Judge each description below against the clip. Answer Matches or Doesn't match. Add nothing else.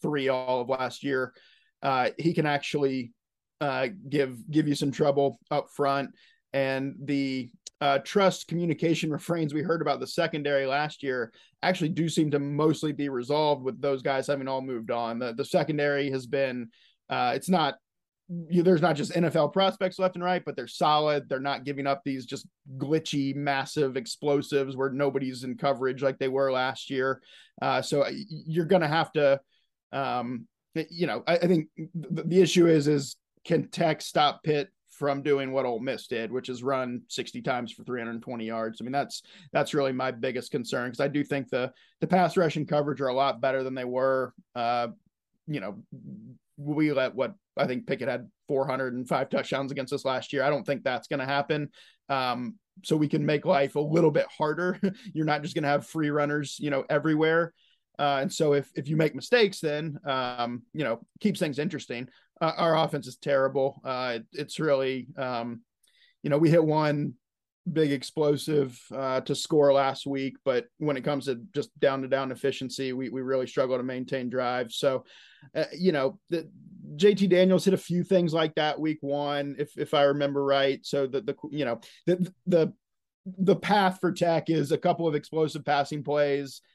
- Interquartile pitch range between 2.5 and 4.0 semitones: Matches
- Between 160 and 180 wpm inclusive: Doesn't match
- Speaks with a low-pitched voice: Doesn't match